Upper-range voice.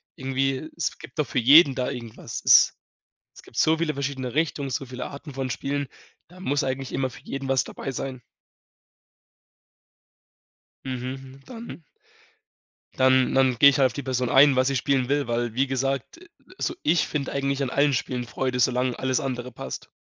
No: low, 135 Hz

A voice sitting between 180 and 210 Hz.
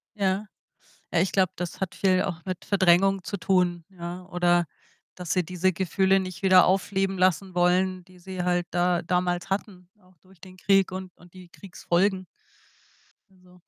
Yes: medium, 185 Hz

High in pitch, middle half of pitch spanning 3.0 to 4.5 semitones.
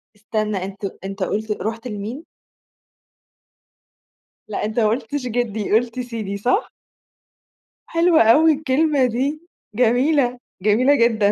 Yes: high, 235 Hz; average, 4.2 semitones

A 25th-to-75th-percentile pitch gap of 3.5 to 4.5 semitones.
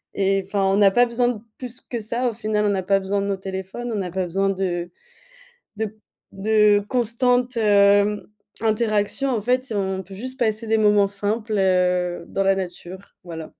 No: average, 2.9 semitones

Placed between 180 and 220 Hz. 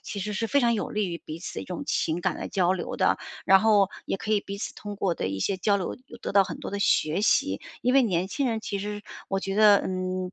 Yes: high, 200 Hz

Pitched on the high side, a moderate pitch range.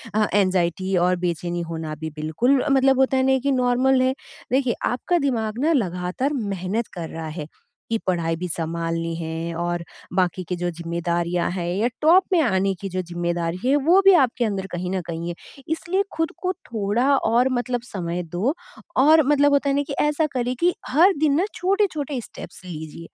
No: high, 215 Hz; wide, 7.8 semitones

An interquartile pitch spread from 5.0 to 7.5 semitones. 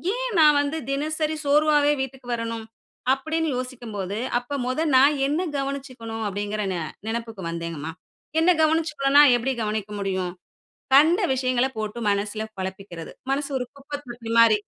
Yes: wide, 5.4 semitones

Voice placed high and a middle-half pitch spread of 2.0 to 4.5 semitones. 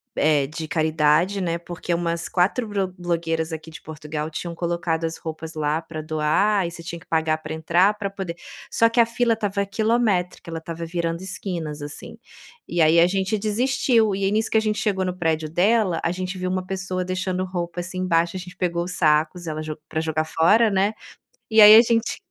No: medium, 175 Hz; average, 3.4 semitones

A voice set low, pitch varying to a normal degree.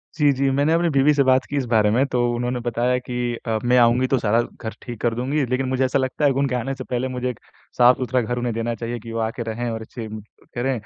No: low, 125 Hz; narrow, 2.1 semitones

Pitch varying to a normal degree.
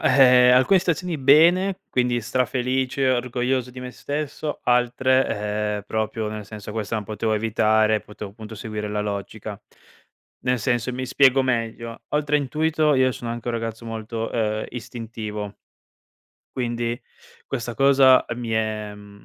Yes: average, 3.2 semitones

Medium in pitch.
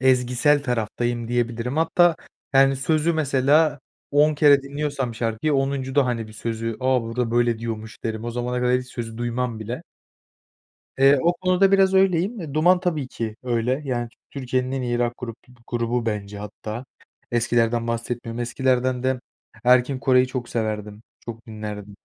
No: low, 125 Hz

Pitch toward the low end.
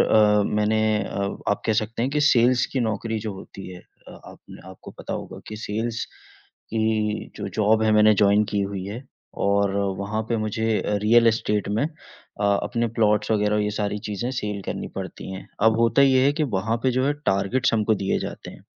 Yes: low, 110 Hz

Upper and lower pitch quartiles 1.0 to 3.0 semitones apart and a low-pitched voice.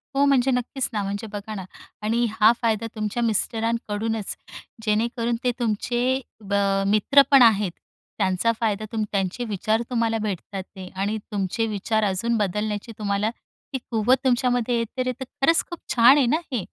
No: average, 2.7 semitones; high, 225 Hz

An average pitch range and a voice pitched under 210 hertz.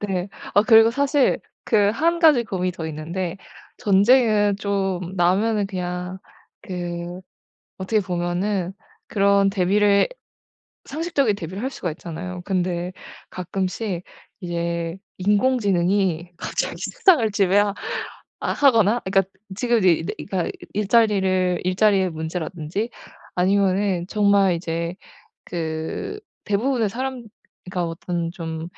Yes: average, 3.0 semitones; high, 190 Hz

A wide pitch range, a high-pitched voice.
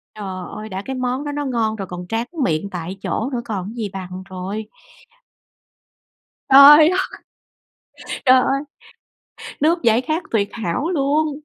Yes: wide, 6.3 semitones; high, 225 Hz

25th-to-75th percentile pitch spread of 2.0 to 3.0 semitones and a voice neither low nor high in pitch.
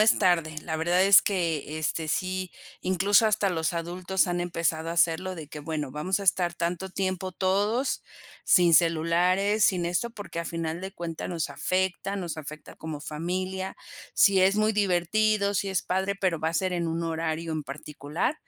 Yes: average, 2.7 semitones; medium, 175 Hz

